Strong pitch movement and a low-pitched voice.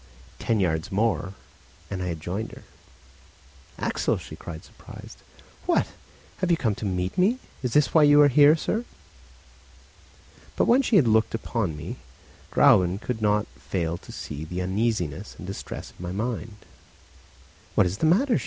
Yes: wide, 8.0 semitones; low, 105 Hz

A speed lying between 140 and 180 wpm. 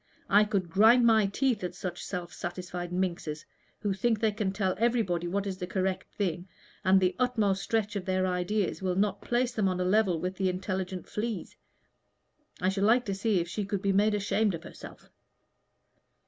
No: average, 190 wpm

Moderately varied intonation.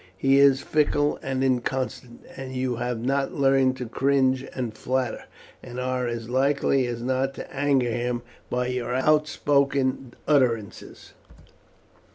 No: narrow, 1.7 semitones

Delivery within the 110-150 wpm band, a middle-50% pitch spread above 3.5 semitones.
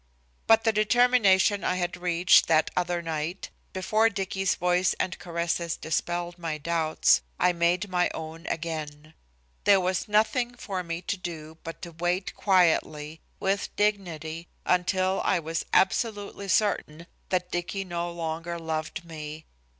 No: average, 140 wpm; average, 2.8 semitones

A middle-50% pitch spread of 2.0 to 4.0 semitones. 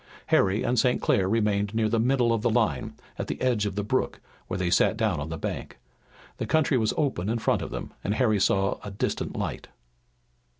Yes: average, 3.2 semitones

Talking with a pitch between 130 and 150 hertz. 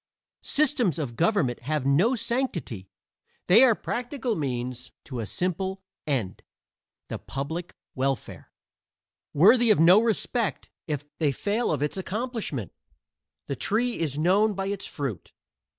No: medium, 175 Hz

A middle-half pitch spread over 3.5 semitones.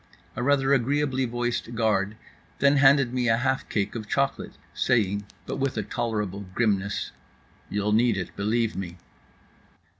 Yes: average, 4.2 semitones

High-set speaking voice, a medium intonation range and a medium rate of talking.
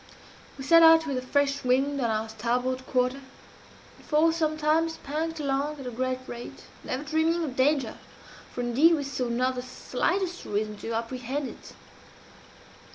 Yes: very high, 270 Hz; average, 3.6 semitones; average, 165 wpm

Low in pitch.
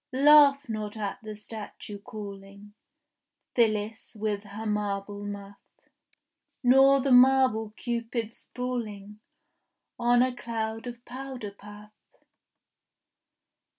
No: high, 220 Hz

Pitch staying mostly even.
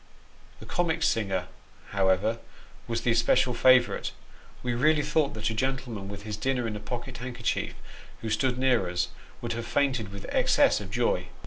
No: average, 3.7 semitones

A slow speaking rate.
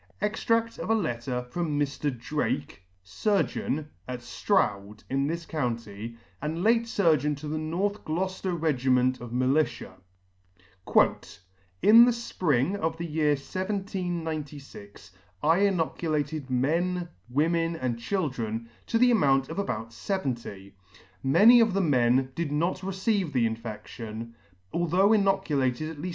Yes: slow, 130 wpm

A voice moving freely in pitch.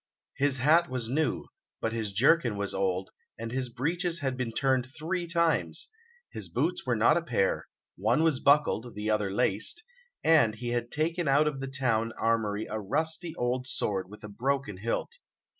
Yes: wide, 6.0 semitones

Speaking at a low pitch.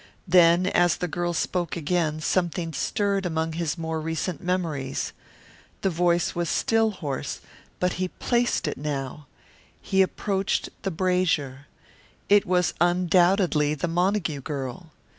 No: medium, 175 Hz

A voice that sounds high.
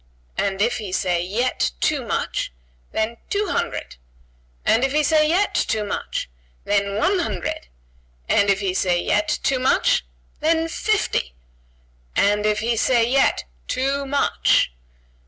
Yes: high, 230 Hz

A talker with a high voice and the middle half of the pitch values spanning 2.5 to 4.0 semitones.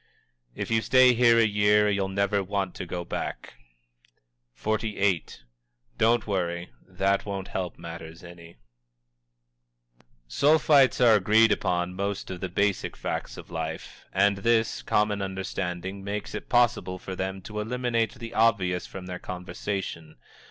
No: low, 100 Hz; average, 3.3 semitones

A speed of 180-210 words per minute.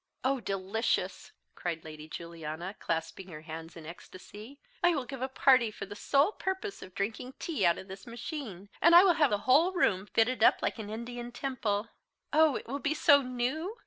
Yes: average, 195 wpm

